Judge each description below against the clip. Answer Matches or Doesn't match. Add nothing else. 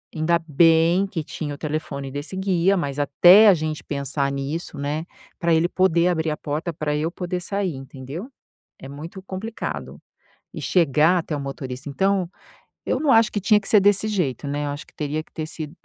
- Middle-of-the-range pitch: Matches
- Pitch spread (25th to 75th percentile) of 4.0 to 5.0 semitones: Matches